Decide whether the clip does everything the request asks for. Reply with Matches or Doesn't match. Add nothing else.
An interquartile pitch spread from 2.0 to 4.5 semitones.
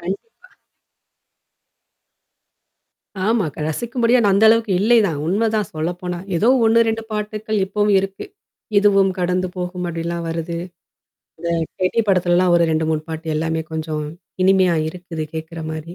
Matches